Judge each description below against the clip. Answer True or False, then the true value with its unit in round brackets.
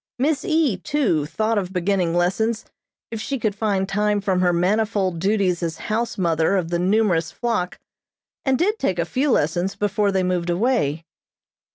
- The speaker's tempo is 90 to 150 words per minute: False (170 wpm)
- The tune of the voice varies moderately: True (4.1 semitones)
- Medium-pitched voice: False (195 Hz)